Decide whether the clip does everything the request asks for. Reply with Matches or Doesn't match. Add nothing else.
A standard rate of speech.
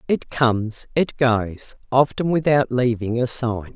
Matches